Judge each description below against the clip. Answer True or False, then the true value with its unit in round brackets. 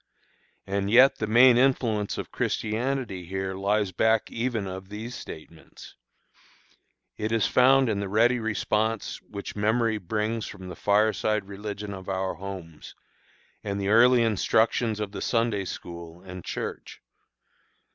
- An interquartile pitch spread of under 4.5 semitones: True (2.8 semitones)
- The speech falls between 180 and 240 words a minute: False (135 wpm)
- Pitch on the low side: True (105 Hz)